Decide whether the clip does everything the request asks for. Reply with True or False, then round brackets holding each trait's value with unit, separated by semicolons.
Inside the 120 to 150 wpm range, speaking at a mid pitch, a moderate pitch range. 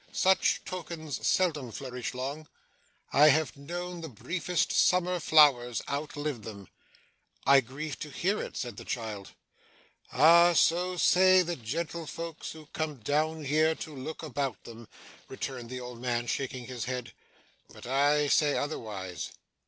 True (140 wpm; 145 Hz; 4.5 semitones)